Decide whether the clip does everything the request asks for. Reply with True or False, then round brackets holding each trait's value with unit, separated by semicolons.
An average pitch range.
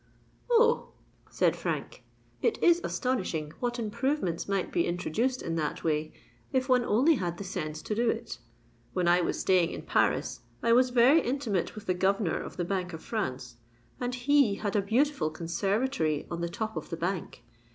False (6.7 semitones)